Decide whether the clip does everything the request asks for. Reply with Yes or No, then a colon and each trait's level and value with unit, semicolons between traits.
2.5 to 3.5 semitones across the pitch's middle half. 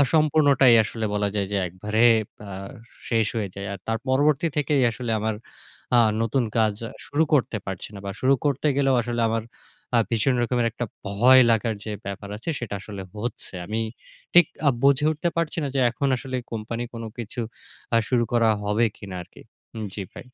No: average, 4.1 semitones